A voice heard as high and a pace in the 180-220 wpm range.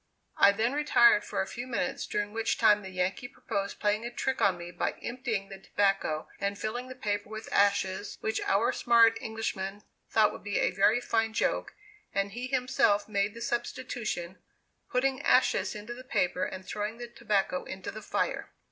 Yes: high, 215 Hz; average, 185 wpm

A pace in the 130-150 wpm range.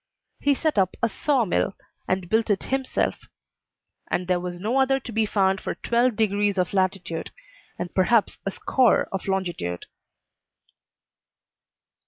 Yes: average, 145 wpm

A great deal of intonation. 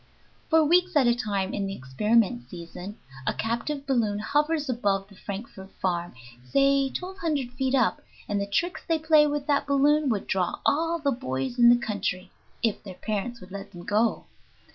Yes: wide, 6.6 semitones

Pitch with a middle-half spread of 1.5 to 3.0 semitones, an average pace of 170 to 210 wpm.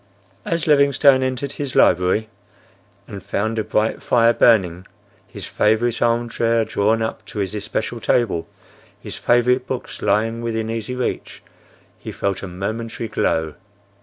No: narrow, 2.5 semitones; average, 140 wpm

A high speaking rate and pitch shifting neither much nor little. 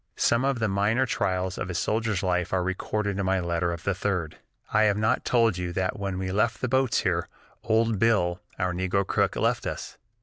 Yes: fast, 210 wpm; average, 3.5 semitones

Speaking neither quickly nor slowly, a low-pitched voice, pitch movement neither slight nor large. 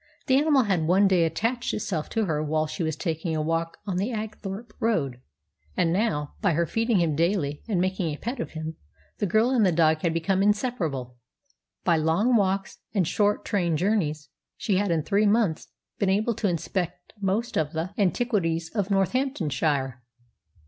No: average, 180 wpm; medium, 185 Hz; average, 4.8 semitones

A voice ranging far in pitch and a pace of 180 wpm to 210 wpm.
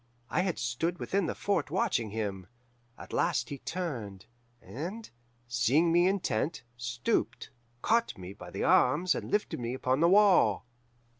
No: wide, 7.7 semitones; average, 150 wpm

